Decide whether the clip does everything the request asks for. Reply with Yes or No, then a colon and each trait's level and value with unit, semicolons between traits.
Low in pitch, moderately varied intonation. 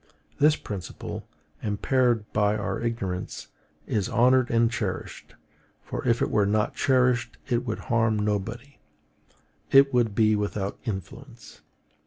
Yes: low, 115 Hz; average, 3.0 semitones